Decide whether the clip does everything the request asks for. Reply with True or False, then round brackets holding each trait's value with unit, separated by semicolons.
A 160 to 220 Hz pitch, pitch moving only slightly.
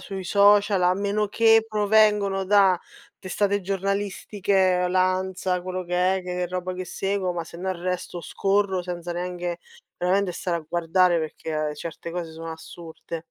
True (185 Hz; 2.1 semitones)